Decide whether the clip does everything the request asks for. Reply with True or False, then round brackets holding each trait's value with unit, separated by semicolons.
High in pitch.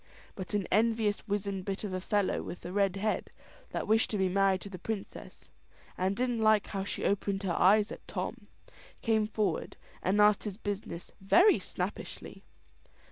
True (200 Hz)